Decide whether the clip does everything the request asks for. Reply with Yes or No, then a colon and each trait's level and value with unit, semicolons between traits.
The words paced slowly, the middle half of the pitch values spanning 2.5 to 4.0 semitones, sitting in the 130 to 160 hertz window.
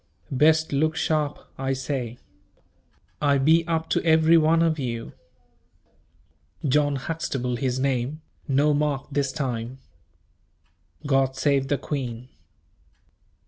Yes: slow, 110 wpm; average, 2.9 semitones; medium, 140 Hz